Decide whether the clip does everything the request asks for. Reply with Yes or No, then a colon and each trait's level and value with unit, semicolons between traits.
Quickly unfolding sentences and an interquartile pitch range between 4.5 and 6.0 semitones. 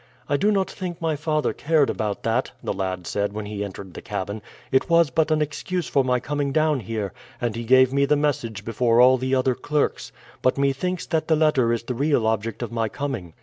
Yes: fast, 225 wpm; average, 5.1 semitones